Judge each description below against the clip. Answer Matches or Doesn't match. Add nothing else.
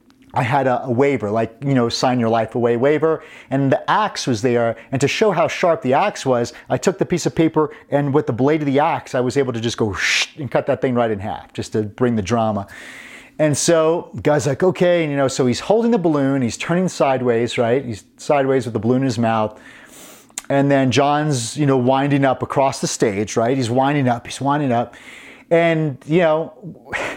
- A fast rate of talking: Matches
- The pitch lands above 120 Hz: Matches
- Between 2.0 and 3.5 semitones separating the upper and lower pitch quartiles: Doesn't match